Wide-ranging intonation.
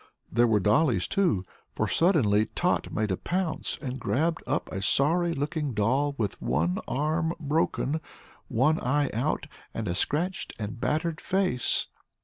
Yes: wide, 6.5 semitones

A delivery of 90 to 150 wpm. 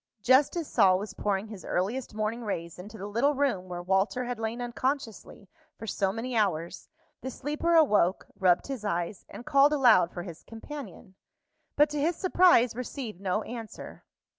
No: average, 170 wpm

